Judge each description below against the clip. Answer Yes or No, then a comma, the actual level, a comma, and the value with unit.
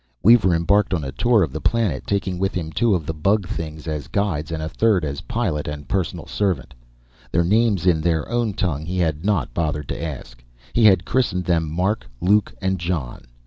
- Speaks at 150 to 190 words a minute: No, fast, 205 wpm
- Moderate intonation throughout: Yes, average, 4.5 semitones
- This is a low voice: Yes, very low, 90 Hz